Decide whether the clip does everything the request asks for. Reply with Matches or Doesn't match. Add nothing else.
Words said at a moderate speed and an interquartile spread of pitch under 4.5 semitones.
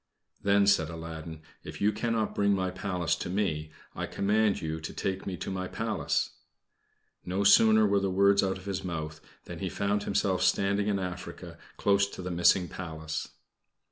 Matches